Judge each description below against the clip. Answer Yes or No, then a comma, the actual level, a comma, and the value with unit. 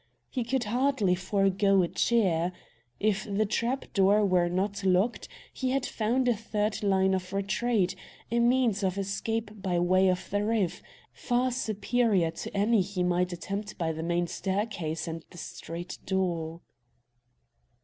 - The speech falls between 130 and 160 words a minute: Yes, average, 150 wpm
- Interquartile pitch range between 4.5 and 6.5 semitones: No, average, 3.5 semitones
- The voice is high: Yes, high, 200 Hz